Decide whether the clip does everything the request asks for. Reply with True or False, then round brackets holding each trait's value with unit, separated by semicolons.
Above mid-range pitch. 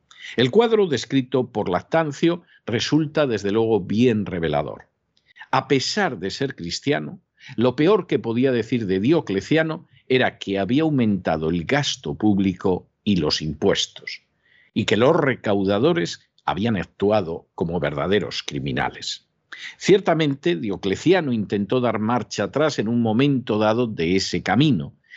False (125 Hz)